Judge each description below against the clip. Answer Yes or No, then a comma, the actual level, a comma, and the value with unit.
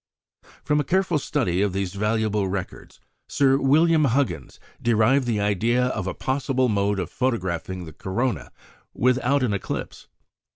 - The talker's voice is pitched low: Yes, low, 115 Hz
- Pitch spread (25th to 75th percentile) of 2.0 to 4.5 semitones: No, average, 5.3 semitones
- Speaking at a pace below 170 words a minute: Yes, average, 140 wpm